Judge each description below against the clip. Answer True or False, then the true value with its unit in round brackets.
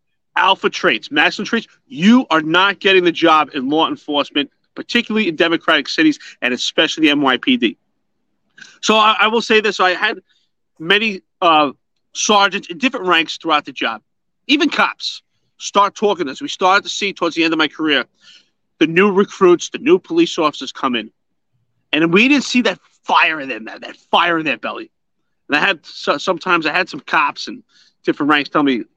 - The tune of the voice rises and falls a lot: True (7.3 semitones)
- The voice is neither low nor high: False (200 Hz)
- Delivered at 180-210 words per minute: True (185 wpm)